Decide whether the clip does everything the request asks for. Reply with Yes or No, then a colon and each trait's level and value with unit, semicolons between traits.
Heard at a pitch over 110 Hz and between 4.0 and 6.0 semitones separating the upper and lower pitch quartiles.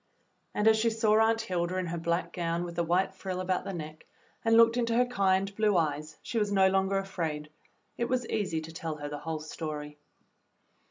Yes: medium, 185 Hz; average, 4.8 semitones